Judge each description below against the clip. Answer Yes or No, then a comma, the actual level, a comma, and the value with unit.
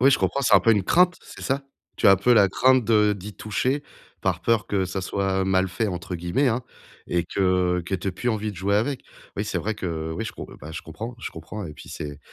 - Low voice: Yes, low, 100 Hz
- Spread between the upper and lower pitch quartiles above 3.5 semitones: Yes, average, 4.0 semitones